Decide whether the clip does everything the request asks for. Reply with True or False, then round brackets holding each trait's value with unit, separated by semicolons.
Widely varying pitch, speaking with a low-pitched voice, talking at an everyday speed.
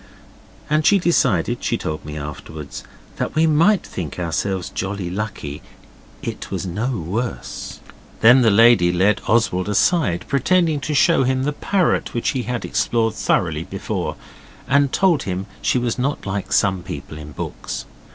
True (7.6 semitones; 110 Hz; 155 wpm)